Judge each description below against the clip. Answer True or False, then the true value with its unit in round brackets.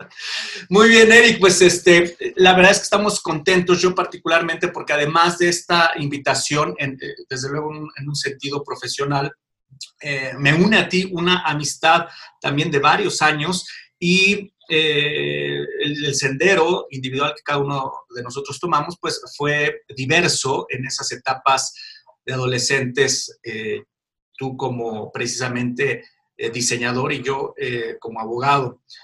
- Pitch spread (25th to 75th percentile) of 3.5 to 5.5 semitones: True (4.9 semitones)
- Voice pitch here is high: False (150 Hz)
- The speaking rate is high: False (135 wpm)